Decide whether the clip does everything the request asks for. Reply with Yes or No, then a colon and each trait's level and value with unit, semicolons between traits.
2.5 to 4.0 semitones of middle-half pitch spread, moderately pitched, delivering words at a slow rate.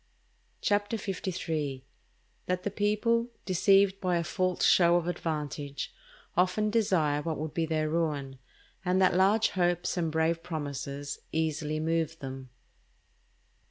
Yes: average, 3.5 semitones; medium, 170 Hz; slow, 125 wpm